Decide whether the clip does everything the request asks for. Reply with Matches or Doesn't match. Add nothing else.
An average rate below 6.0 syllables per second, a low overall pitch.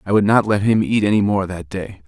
Matches